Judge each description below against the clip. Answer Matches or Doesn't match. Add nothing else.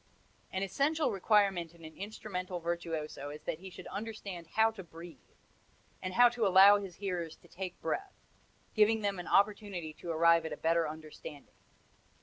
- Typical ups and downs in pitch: Matches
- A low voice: Doesn't match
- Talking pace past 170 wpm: Doesn't match